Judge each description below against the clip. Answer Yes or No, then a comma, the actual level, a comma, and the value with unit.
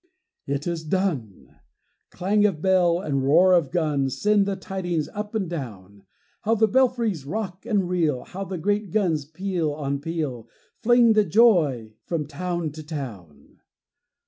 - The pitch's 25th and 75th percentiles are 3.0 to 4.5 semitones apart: No, wide, 5.6 semitones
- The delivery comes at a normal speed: Yes, average, 150 wpm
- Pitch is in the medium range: Yes, medium, 170 Hz